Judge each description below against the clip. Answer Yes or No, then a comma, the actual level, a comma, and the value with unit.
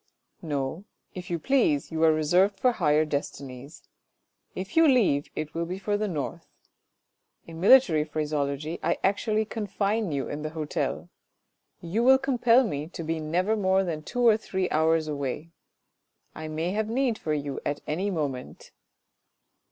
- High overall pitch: No, medium, 165 Hz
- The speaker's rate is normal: Yes, average, 160 wpm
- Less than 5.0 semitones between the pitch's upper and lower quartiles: No, wide, 5.4 semitones